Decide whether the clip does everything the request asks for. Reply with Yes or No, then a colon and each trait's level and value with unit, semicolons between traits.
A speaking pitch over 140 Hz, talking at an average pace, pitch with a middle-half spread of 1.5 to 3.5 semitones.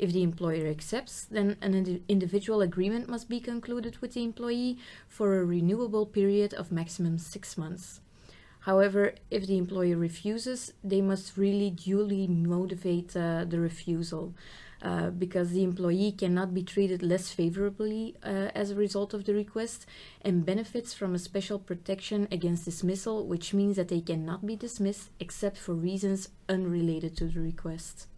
Yes: high, 190 Hz; average, 160 wpm; average, 2.9 semitones